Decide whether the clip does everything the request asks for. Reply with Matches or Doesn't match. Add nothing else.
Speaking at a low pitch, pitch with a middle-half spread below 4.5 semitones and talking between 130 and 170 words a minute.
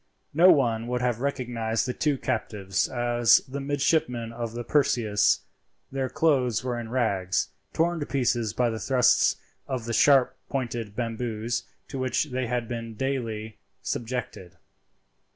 Matches